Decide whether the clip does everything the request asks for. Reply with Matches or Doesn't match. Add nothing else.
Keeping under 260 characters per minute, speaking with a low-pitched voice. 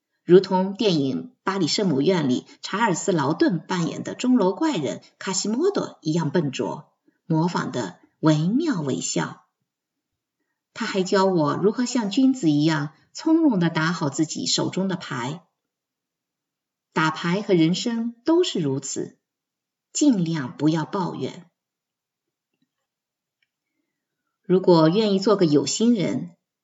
Doesn't match